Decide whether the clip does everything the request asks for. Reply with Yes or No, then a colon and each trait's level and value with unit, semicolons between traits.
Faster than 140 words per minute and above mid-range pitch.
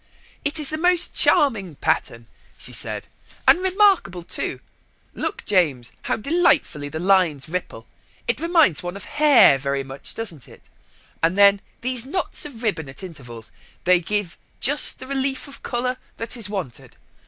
Yes: average, 155 wpm; high, 200 Hz